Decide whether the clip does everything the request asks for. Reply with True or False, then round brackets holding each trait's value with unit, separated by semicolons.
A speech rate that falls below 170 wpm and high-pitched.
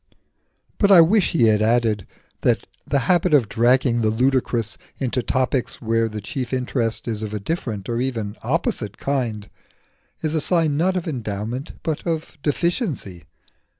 False (155 wpm; 125 Hz)